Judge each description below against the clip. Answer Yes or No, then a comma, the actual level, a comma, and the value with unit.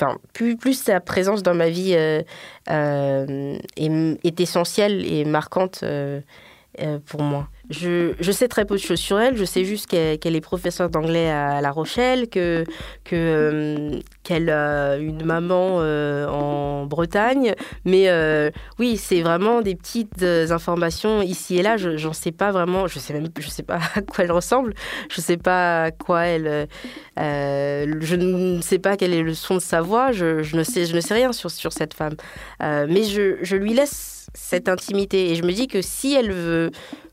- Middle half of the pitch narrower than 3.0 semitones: No, average, 3.7 semitones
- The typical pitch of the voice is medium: Yes, medium, 175 Hz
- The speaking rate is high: No, average, 200 wpm